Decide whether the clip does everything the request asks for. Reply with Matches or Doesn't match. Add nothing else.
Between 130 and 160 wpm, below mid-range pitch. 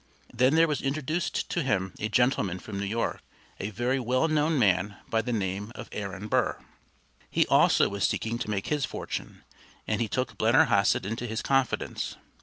Doesn't match